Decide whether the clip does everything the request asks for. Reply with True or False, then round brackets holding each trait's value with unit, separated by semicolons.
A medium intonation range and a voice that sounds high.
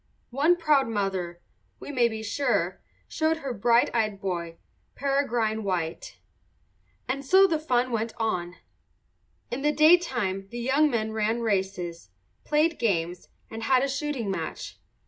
False (6.1 semitones; 235 Hz)